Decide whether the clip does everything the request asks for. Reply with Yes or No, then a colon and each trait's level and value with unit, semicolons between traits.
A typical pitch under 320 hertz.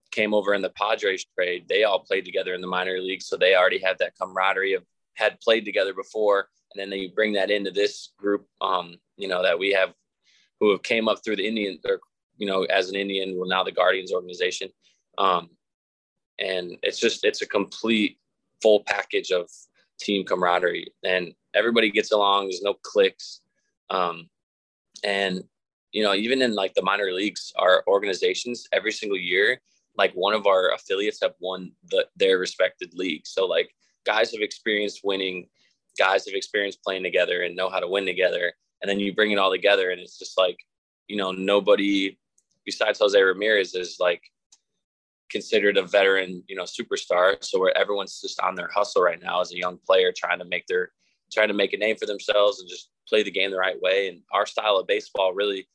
No: very high, 350 Hz